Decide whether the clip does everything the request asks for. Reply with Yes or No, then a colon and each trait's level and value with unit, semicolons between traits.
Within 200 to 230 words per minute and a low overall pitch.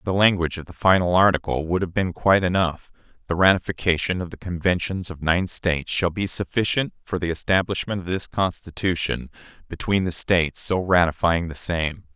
No: average, 175 wpm; very low, 90 Hz